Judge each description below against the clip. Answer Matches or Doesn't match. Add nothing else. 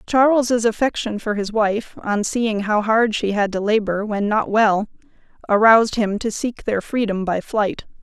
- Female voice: Matches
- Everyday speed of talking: Matches